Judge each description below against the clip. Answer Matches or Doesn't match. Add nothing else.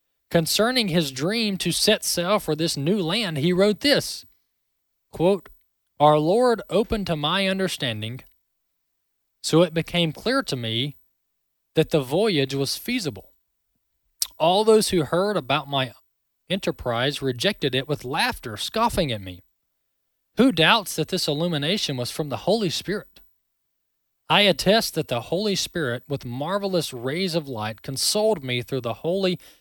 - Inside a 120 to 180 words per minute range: Matches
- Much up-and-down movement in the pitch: Matches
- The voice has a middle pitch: Matches